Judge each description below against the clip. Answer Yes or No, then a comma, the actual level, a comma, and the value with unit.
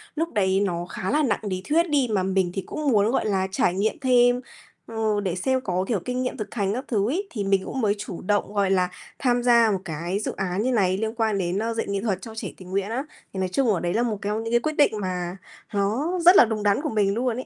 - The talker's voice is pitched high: Yes, high, 210 Hz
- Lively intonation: No, average, 4.2 semitones